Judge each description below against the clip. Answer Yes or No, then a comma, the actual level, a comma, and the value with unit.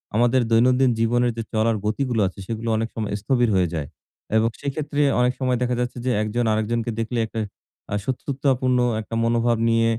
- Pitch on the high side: No, low, 120 Hz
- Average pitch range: No, narrow, 1.9 semitones